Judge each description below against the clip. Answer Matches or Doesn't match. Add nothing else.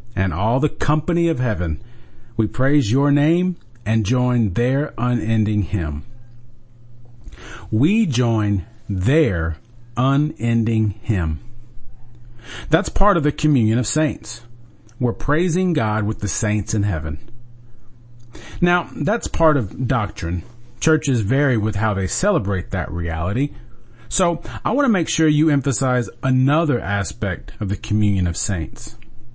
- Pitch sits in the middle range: Doesn't match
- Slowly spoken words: Matches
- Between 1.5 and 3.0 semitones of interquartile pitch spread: Doesn't match